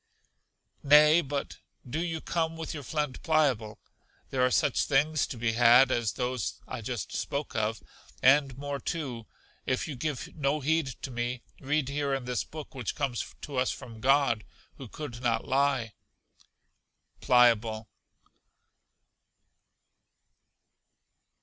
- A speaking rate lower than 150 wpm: Yes, slow, 135 wpm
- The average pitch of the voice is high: No, low, 135 Hz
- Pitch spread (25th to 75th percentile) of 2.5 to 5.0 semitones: Yes, average, 3.6 semitones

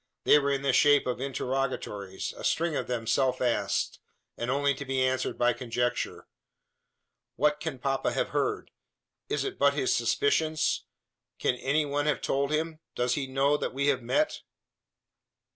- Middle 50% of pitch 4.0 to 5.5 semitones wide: No, average, 2.8 semitones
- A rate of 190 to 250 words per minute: No, average, 165 wpm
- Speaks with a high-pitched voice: No, low, 135 Hz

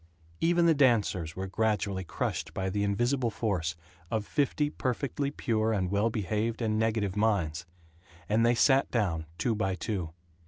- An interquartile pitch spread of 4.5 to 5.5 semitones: No, average, 3.9 semitones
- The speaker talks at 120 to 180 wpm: Yes, average, 155 wpm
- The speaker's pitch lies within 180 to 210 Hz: No, low, 110 Hz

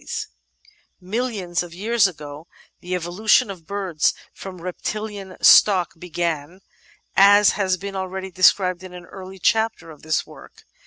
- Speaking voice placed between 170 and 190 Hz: Yes, medium, 185 Hz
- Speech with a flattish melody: Yes, narrow, 2.3 semitones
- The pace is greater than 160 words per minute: No, average, 150 wpm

